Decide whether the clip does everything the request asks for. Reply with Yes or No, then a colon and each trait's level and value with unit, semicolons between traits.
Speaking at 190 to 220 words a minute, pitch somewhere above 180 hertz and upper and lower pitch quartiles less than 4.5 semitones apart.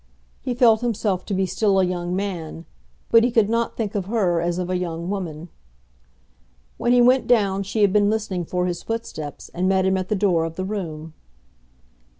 Yes: average, 200 wpm; high, 190 Hz; average, 3.5 semitones